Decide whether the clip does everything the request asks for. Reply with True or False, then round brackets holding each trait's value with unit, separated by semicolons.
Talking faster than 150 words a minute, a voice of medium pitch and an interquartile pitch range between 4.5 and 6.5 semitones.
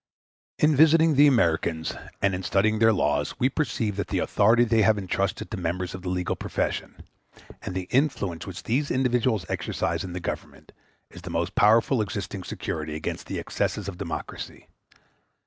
False (170 wpm; 100 Hz; 5.0 semitones)